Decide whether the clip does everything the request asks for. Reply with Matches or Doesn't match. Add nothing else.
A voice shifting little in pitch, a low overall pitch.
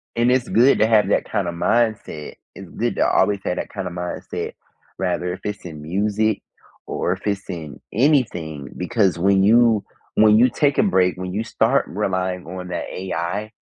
Doesn't match